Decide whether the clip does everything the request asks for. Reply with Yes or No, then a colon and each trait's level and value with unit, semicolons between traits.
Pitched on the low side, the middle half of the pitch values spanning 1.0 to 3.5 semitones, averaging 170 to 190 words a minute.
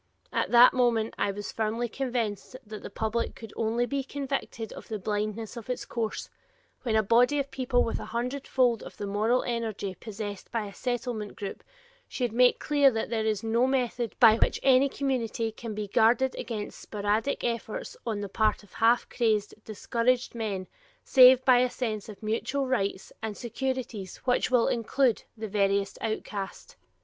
No: high, 230 Hz; average, 2.8 semitones; average, 175 wpm